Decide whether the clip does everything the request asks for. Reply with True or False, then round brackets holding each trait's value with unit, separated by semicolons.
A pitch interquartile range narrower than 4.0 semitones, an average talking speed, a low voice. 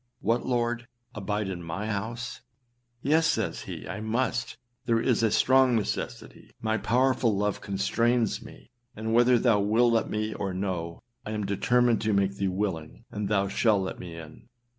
True (3.4 semitones; 170 wpm; 110 Hz)